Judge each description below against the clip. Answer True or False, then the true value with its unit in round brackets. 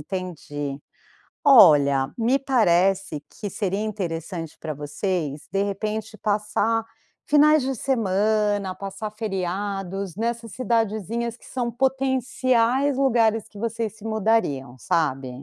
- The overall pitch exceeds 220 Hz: False (210 Hz)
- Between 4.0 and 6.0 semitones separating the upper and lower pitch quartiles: True (4.4 semitones)